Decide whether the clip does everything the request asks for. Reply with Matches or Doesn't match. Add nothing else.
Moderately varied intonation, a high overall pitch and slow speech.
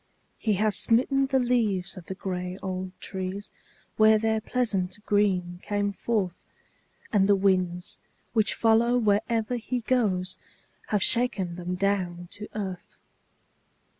Matches